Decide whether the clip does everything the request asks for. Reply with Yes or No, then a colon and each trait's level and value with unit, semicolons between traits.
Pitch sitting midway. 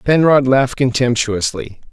No: low, 130 Hz